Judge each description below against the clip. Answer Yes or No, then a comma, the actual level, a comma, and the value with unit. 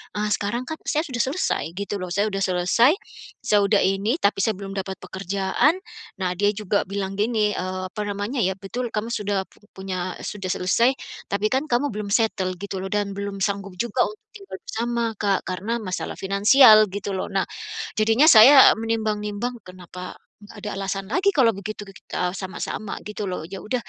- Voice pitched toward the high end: Yes, high, 205 Hz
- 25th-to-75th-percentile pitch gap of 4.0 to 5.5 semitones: No, average, 2.9 semitones